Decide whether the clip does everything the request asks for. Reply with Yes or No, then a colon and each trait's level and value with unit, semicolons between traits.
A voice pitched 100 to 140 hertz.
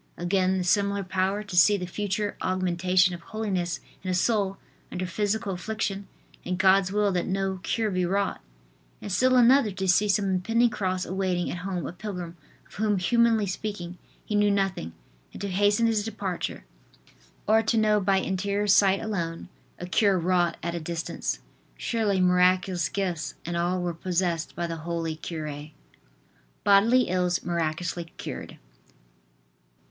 No: high, 190 Hz